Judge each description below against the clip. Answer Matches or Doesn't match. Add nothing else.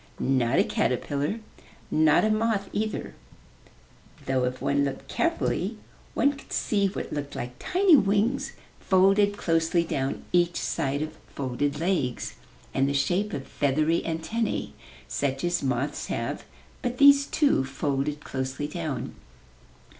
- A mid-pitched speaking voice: Matches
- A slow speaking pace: Matches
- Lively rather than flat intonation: Matches